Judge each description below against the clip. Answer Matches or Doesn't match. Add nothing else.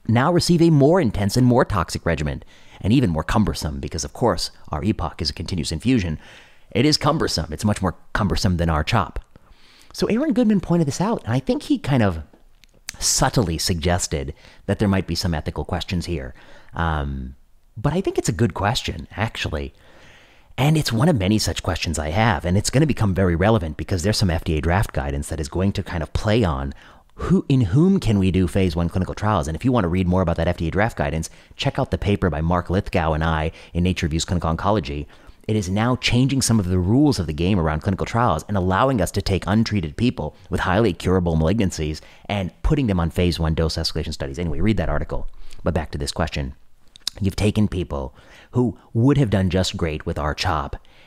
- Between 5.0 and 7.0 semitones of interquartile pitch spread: Matches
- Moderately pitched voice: Doesn't match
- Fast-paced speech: Matches